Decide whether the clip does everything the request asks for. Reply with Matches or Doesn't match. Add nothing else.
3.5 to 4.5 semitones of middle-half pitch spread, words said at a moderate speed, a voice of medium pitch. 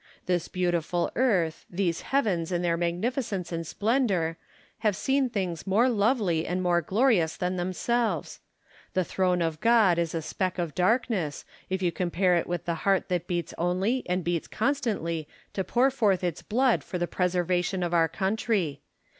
Matches